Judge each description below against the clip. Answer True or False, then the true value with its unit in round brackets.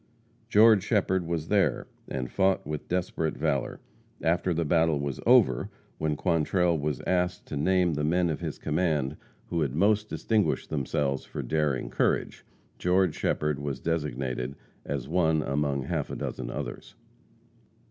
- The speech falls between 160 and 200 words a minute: False (145 wpm)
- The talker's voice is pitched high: False (80 Hz)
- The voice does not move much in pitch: False (4.0 semitones)